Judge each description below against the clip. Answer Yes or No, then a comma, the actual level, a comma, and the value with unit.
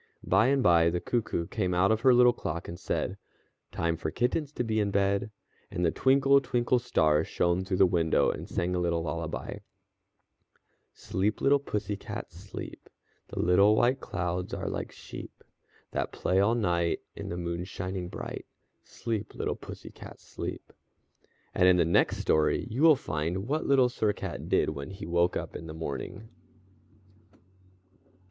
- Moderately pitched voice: No, very low, 95 Hz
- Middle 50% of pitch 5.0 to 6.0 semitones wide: Yes, wide, 5.5 semitones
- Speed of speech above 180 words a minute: No, average, 170 wpm